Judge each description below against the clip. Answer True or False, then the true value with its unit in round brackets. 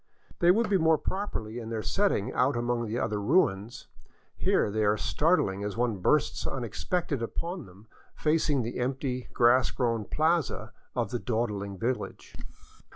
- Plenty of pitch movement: True (5.8 semitones)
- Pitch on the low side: True (120 Hz)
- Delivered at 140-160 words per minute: True (155 wpm)